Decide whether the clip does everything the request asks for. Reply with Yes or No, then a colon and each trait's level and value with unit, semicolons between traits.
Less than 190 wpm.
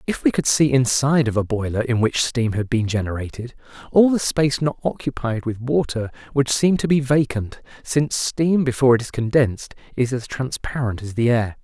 No: average, 195 wpm